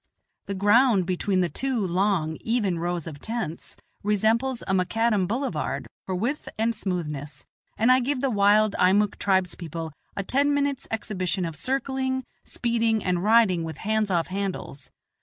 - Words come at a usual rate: Yes, average, 155 wpm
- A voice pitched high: Yes, high, 200 Hz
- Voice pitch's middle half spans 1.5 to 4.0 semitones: No, average, 4.7 semitones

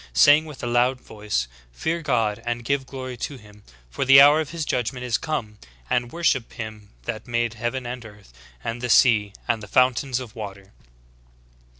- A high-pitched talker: No, low, 120 Hz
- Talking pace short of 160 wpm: No, average, 185 wpm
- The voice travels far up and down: No, average, 3.5 semitones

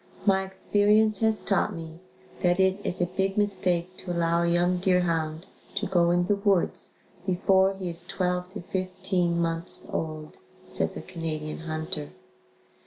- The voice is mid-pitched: Yes, medium, 180 Hz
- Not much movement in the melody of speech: Yes, narrow, 2.1 semitones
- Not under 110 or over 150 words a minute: No, average, 160 wpm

